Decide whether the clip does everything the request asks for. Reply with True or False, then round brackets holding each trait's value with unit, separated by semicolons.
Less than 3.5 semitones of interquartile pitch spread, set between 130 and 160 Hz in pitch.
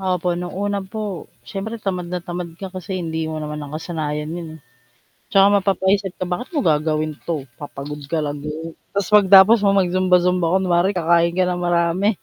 False (3.1 semitones; 180 Hz)